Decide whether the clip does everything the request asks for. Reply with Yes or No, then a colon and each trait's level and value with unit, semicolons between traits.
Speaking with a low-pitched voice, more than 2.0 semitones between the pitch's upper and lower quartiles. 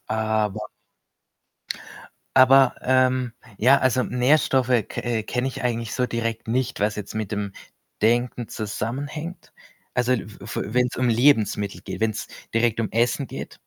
Yes: low, 120 Hz; average, 2.7 semitones